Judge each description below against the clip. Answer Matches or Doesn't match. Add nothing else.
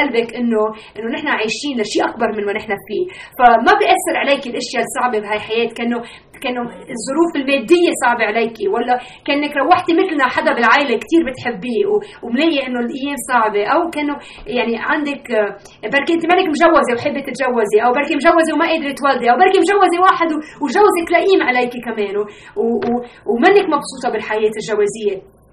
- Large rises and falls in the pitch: Matches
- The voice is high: Matches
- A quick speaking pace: Matches